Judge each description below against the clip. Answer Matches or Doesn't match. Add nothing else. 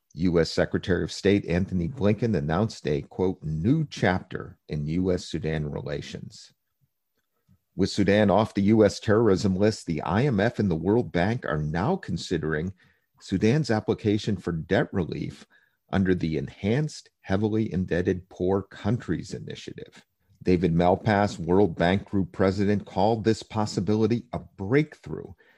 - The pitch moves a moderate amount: Matches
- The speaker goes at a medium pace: Doesn't match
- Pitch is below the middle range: Matches